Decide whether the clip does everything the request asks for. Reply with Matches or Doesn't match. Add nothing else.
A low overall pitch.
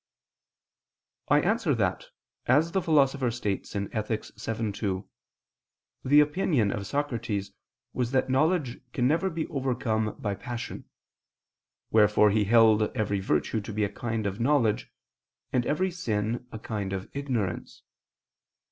Matches